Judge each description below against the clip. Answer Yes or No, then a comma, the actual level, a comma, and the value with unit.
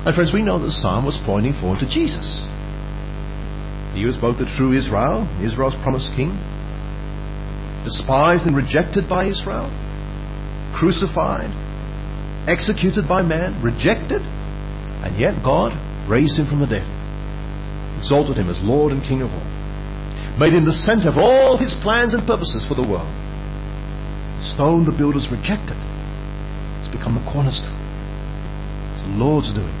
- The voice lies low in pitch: No, medium, 145 Hz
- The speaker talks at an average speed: Yes, average, 145 wpm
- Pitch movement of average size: No, wide, 5.7 semitones